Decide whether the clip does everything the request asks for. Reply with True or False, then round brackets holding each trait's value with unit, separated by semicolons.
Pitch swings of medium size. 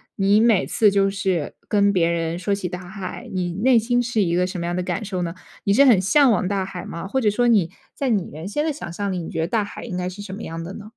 True (3.2 semitones)